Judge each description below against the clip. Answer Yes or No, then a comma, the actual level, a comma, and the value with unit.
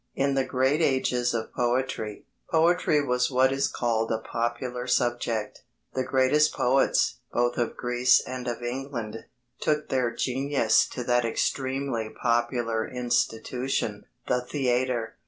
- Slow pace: Yes, slow, 130 wpm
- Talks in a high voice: No, low, 125 Hz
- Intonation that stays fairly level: Yes, narrow, 2.0 semitones